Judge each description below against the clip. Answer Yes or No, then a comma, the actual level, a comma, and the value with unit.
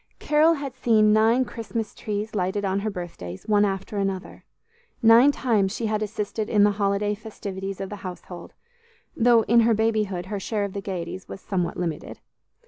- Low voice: No, high, 205 Hz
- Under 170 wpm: No, average, 175 wpm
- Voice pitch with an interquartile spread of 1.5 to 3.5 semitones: Yes, narrow, 2.5 semitones